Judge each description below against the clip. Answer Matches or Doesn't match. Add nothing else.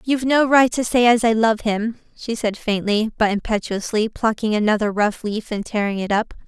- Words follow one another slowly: Doesn't match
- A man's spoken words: Doesn't match